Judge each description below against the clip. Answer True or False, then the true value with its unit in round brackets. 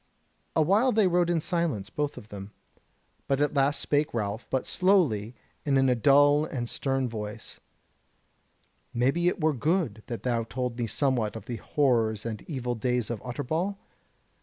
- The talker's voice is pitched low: True (130 Hz)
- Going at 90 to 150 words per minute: False (165 wpm)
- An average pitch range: True (4.9 semitones)